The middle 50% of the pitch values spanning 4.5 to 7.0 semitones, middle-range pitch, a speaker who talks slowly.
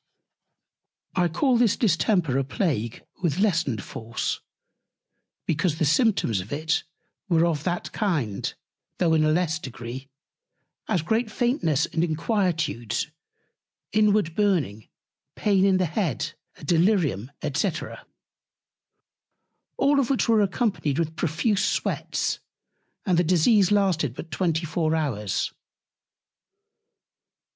Yes: average, 5.2 semitones; medium, 170 Hz; slow, 110 wpm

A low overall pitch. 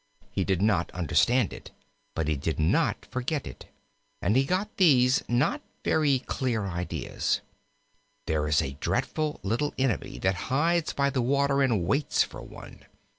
Yes: low, 125 Hz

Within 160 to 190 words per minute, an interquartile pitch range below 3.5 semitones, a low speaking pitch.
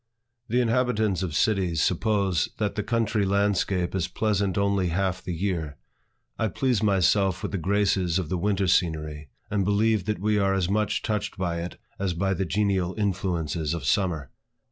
Yes: average, 170 wpm; average, 2.8 semitones; very low, 95 Hz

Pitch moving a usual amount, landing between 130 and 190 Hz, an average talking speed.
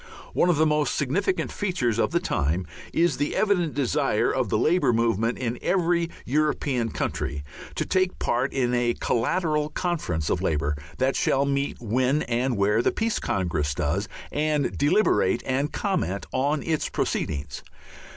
No: wide, 5.7 semitones; low, 135 Hz; average, 155 wpm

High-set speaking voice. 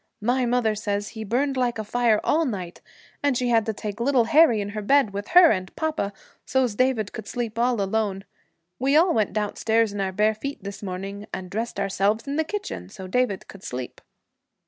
Yes: high, 220 Hz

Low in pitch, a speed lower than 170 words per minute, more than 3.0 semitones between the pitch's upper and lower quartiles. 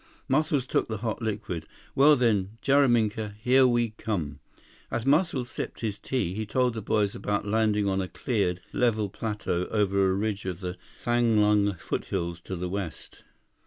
Yes: low, 105 Hz; average, 160 wpm; average, 3.6 semitones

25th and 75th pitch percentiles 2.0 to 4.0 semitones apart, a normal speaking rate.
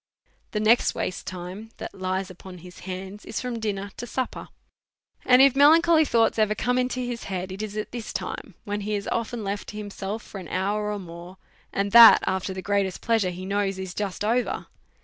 No: average, 3.3 semitones; fast, 210 wpm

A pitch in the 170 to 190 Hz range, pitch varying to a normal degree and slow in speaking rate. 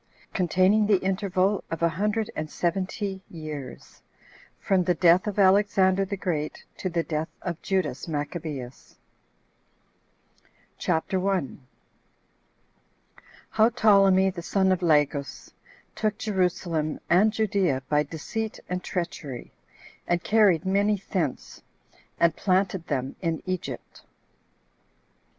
Yes: medium, 185 Hz; average, 3.5 semitones; slow, 110 wpm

